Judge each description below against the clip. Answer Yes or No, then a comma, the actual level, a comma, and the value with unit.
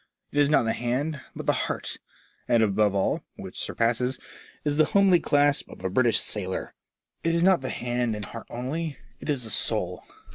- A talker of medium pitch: No, low, 125 Hz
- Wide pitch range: No, average, 4.6 semitones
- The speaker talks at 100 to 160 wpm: No, fast, 205 wpm